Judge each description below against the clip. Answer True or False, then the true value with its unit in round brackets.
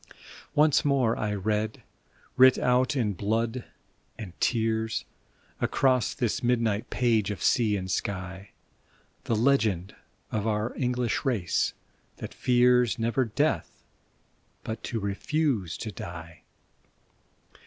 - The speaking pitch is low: True (110 Hz)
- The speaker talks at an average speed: False (110 wpm)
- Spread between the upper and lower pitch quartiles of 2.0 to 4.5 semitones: True (3.4 semitones)